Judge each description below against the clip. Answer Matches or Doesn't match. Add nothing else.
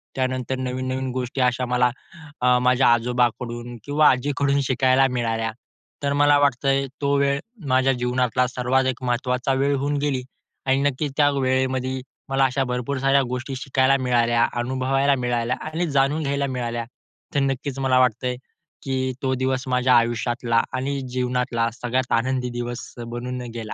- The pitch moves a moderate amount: Doesn't match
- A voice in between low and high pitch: Doesn't match